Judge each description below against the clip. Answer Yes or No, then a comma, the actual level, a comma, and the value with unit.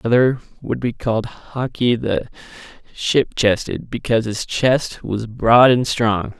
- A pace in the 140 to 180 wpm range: Yes, average, 150 wpm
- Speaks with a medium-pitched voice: No, low, 120 Hz